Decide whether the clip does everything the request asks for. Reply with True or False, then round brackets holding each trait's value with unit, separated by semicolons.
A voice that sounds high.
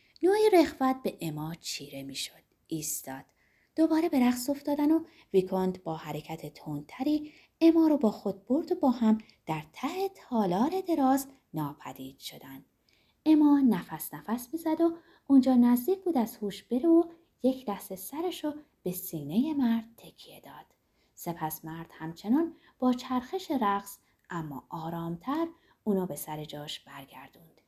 True (240 Hz)